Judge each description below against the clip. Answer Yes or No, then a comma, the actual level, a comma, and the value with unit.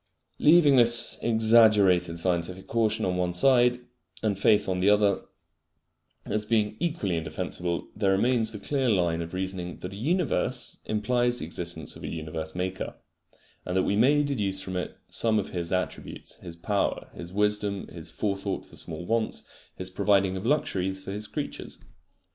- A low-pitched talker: Yes, low, 100 Hz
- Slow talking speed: No, average, 165 wpm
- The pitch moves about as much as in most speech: Yes, average, 3.9 semitones